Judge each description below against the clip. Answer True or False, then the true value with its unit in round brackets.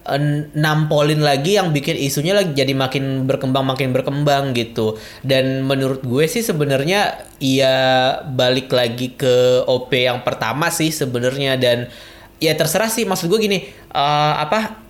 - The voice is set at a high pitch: False (135 Hz)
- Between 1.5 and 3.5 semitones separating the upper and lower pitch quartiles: True (3.2 semitones)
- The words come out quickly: True (150 wpm)